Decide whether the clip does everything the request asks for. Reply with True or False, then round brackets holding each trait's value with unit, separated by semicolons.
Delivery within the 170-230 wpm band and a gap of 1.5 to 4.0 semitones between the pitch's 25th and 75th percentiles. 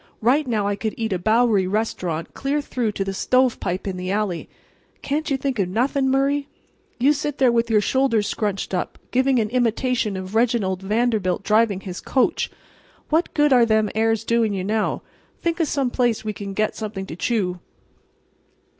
False (180 wpm; 4.4 semitones)